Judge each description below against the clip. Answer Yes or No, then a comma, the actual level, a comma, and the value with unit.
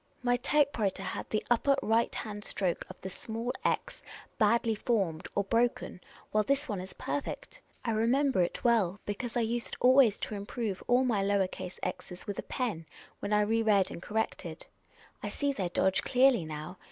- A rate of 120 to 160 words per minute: No, average, 185 wpm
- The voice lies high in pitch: Yes, high, 220 Hz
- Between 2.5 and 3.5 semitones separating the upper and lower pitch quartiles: No, average, 4.0 semitones